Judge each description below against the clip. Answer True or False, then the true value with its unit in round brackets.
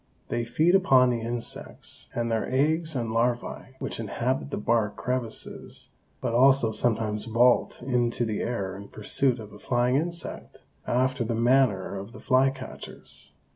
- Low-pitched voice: True (120 Hz)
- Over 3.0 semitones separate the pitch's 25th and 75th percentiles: False (2.5 semitones)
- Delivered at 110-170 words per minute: True (150 wpm)